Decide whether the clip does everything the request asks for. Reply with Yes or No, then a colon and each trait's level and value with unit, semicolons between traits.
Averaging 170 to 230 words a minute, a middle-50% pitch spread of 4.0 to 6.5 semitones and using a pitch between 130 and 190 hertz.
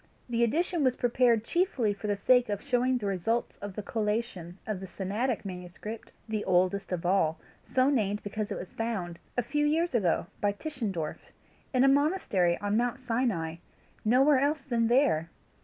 No: average, 175 wpm; average, 4.7 semitones; high, 225 Hz